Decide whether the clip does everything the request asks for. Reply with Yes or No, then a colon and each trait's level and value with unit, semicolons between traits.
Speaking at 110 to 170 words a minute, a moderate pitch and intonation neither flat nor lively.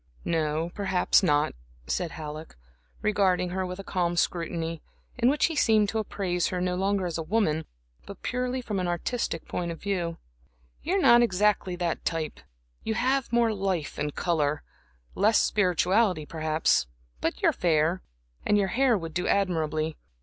Yes: average, 165 wpm; medium, 180 Hz; average, 4.1 semitones